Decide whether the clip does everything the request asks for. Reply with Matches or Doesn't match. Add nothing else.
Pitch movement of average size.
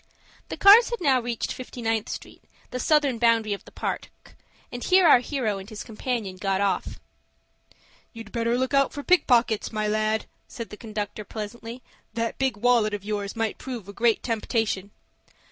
Matches